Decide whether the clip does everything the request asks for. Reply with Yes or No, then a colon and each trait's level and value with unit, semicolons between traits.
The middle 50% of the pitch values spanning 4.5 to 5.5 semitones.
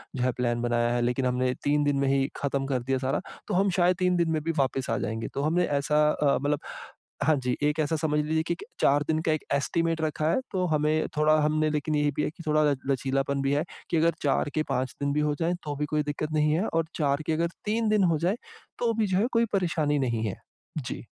No: average, 2.9 semitones